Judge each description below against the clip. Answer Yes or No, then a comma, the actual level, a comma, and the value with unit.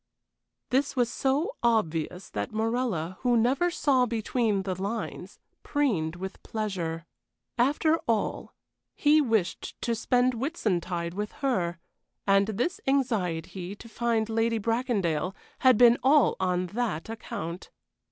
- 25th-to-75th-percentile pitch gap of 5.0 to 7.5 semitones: Yes, average, 5.3 semitones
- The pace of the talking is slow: Yes, slow, 125 wpm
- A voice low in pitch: No, high, 225 Hz